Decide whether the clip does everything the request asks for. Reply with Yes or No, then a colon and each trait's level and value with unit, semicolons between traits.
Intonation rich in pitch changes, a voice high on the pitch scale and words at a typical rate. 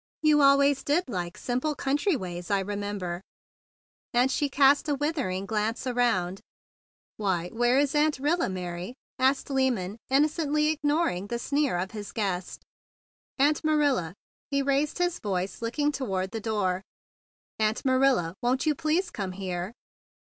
Yes: wide, 7.1 semitones; high, 245 Hz; average, 145 wpm